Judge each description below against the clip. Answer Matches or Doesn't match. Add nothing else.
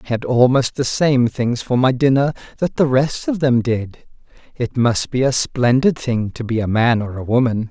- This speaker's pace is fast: Matches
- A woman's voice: Doesn't match